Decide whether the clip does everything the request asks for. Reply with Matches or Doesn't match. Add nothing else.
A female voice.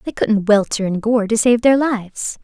Matches